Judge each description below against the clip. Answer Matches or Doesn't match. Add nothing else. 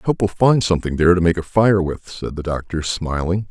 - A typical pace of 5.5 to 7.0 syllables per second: Matches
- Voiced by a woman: Doesn't match